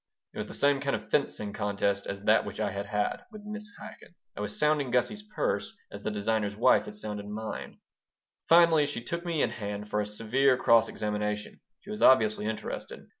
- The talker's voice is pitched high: No, low, 110 Hz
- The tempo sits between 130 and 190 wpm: No, average, 200 wpm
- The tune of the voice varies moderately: No, wide, 5.9 semitones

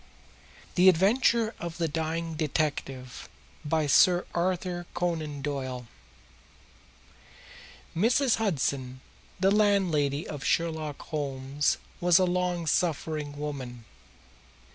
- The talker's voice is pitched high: No, medium, 160 Hz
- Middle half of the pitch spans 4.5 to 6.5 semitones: No, average, 3.9 semitones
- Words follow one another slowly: Yes, slow, 95 wpm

